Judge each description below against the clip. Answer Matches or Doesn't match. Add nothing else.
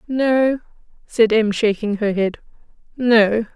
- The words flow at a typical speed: Doesn't match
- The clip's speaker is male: Doesn't match